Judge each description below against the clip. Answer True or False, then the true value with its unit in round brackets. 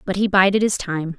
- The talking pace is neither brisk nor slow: False (255 wpm)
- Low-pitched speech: False (190 Hz)